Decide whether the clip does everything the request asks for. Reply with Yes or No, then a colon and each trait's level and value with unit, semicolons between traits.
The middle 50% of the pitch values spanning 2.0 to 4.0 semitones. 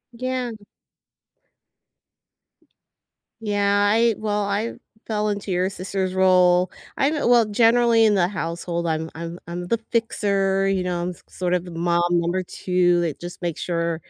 Yes: average, 3.2 semitones